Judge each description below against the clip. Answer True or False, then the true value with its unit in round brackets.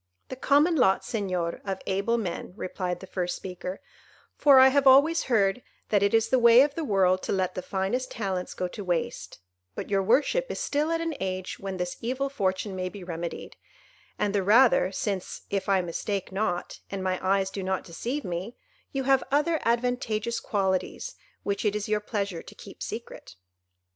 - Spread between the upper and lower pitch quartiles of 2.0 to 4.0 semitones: False (5.1 semitones)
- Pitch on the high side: True (200 Hz)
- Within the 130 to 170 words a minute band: False (190 wpm)